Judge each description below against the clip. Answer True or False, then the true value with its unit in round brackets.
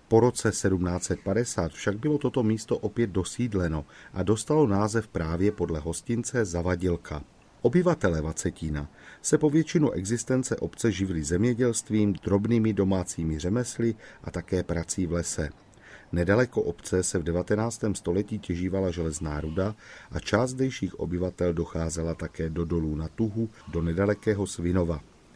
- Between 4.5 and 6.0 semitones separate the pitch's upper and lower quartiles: True (4.9 semitones)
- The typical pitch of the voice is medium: False (95 Hz)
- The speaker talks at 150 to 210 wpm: False (130 wpm)